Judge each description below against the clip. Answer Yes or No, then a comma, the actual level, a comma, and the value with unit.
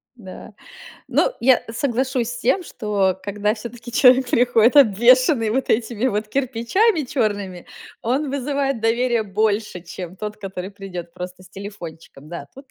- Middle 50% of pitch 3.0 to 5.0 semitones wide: Yes, average, 4.3 semitones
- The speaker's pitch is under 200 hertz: No, high, 225 Hz